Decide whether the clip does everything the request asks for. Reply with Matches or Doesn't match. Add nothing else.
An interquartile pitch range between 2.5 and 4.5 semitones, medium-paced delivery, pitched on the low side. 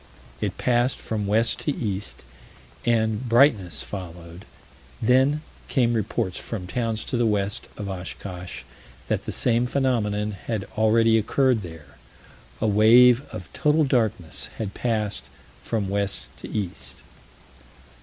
Doesn't match